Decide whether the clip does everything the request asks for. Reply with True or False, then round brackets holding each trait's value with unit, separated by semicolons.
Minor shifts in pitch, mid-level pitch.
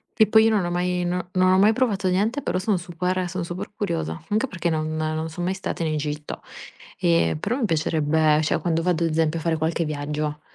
False (3.1 semitones; 170 Hz)